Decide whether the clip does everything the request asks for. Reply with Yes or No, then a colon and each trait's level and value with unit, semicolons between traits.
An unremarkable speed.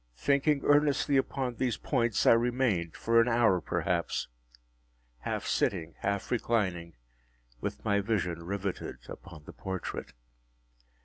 No: slow, 120 wpm